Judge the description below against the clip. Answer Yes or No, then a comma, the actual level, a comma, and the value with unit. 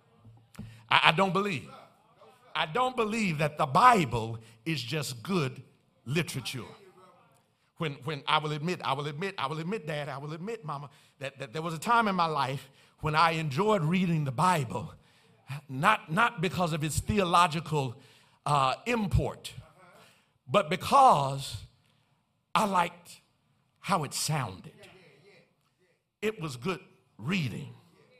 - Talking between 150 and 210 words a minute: No, slow, 135 wpm